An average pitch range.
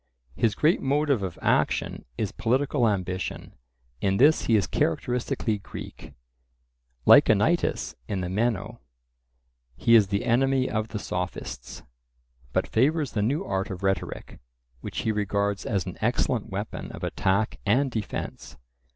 Yes: average, 4.4 semitones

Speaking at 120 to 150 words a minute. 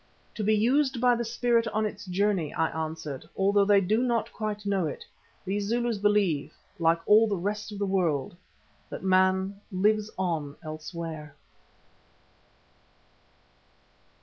Yes: average, 140 wpm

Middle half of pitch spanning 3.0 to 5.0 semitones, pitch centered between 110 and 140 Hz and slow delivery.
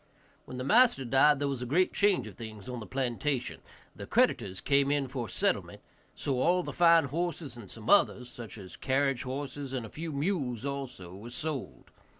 No: average, 3.6 semitones; low, 135 Hz; average, 195 wpm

